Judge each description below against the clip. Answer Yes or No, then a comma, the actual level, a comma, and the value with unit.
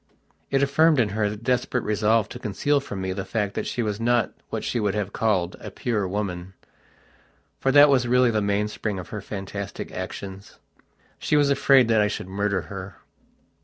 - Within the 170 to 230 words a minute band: Yes, average, 190 wpm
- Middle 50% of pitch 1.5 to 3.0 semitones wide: No, average, 3.7 semitones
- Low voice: Yes, low, 105 Hz